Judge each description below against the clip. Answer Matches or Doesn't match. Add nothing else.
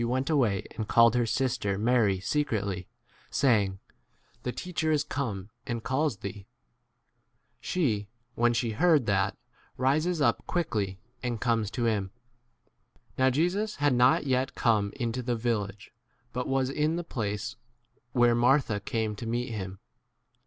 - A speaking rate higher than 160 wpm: Doesn't match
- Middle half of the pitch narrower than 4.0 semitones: Doesn't match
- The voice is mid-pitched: Doesn't match